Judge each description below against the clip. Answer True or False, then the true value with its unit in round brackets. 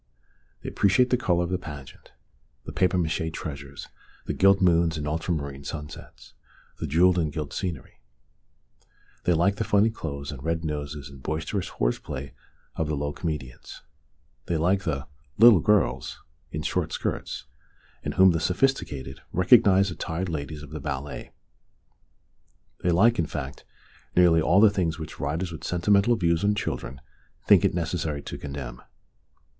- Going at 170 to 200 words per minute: False (160 wpm)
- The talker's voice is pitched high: False (80 Hz)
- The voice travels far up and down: False (4.1 semitones)